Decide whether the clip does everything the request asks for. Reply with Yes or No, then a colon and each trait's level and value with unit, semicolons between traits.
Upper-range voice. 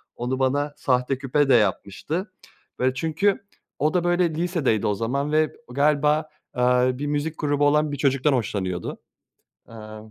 No: medium, 140 Hz